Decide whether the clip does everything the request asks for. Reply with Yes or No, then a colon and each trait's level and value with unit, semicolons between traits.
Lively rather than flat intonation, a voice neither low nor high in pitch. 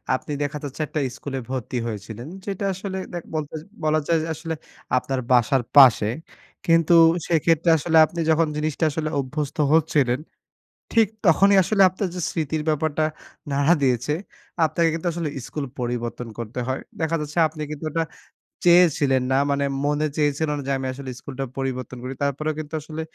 No: average, 3.5 semitones; medium, 150 Hz